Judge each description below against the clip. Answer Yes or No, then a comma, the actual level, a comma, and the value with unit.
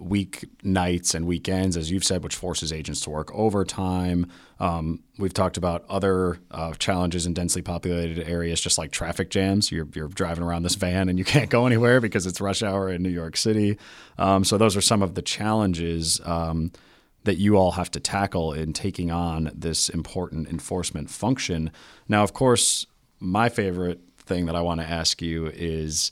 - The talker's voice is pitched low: Yes, very low, 90 Hz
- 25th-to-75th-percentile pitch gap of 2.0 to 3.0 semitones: Yes, narrow, 2.6 semitones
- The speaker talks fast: No, average, 190 wpm